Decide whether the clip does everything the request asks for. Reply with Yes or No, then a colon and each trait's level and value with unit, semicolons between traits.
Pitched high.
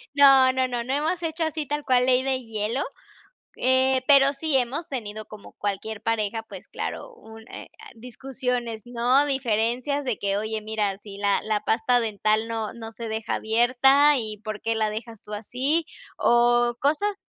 Yes: high, 240 Hz